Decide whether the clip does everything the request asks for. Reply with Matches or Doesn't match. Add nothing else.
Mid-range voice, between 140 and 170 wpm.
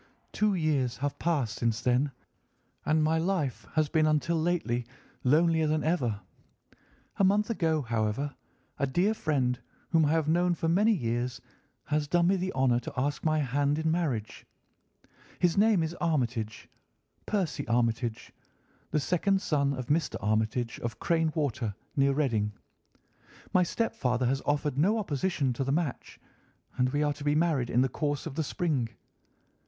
Matches